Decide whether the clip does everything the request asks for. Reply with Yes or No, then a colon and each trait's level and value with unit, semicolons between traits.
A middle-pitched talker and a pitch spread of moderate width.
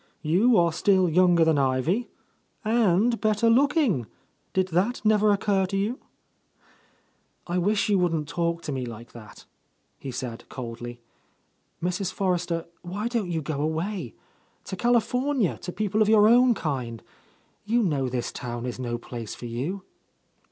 No: medium, 180 Hz; wide, 7.8 semitones